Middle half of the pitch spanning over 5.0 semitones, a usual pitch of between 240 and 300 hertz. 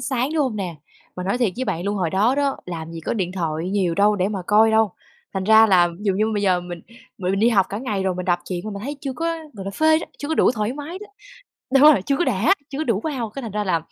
No: wide, 5.4 semitones; high, 205 Hz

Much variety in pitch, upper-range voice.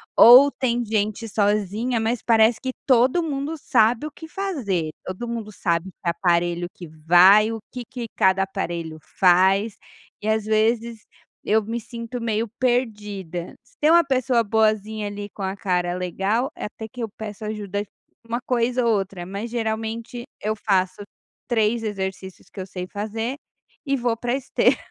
No: average, 3.7 semitones; high, 220 Hz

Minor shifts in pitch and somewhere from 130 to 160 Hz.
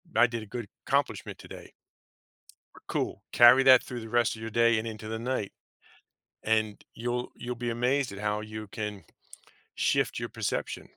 No: narrow, 2.0 semitones; low, 115 Hz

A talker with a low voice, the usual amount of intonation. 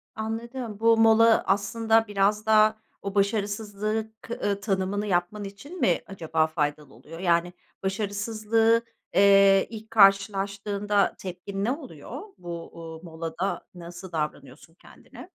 No: high, 200 Hz; average, 3.4 semitones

